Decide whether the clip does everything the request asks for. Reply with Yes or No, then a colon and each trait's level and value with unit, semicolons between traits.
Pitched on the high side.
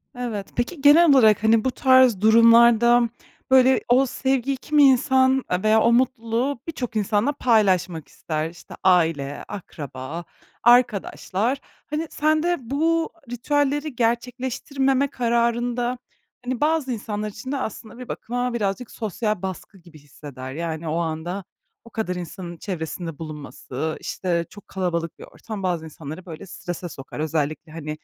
Yes: high, 225 Hz